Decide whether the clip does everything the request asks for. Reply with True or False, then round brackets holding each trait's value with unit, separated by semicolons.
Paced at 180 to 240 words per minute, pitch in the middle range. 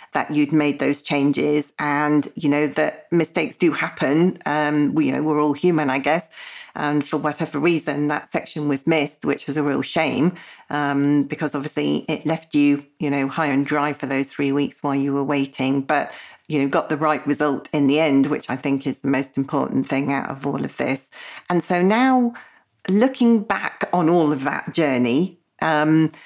True (200 wpm; 150 Hz)